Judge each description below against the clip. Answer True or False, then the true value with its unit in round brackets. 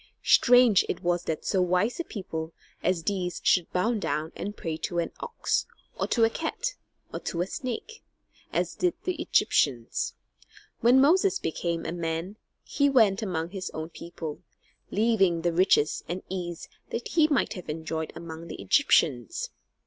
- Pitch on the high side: False (180 Hz)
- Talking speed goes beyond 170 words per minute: False (165 wpm)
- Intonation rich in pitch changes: True (6.0 semitones)